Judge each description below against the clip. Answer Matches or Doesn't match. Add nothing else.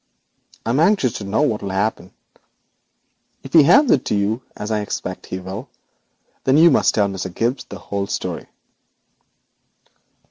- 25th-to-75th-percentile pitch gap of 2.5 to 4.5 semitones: Doesn't match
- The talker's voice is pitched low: Matches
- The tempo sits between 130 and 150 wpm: Doesn't match